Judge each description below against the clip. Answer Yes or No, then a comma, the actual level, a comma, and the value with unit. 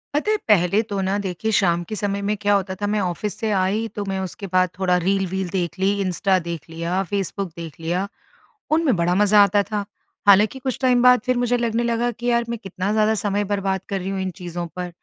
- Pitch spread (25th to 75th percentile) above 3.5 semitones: No, average, 2.7 semitones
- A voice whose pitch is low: No, high, 195 Hz